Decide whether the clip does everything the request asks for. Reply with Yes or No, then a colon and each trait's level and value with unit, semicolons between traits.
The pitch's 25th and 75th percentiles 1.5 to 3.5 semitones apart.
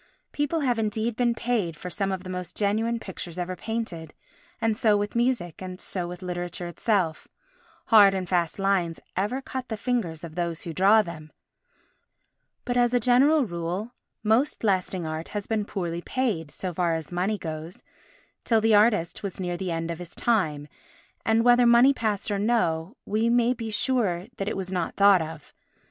No: average, 4.8 semitones